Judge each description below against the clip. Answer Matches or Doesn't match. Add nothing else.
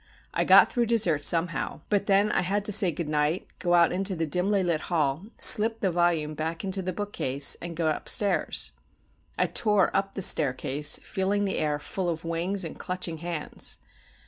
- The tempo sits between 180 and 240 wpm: Matches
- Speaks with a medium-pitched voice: Matches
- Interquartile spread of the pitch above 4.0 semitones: Doesn't match